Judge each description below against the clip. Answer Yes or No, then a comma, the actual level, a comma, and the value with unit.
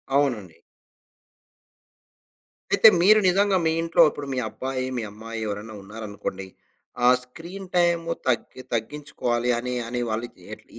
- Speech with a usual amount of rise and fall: No, wide, 6.9 semitones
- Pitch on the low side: Yes, low, 125 Hz